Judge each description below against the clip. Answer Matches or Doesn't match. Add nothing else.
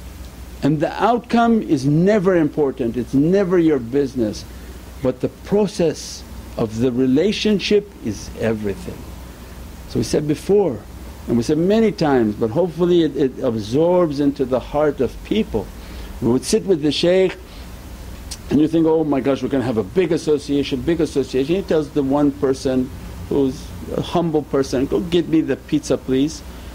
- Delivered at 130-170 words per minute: Matches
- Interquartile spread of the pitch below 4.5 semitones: Doesn't match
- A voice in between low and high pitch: Matches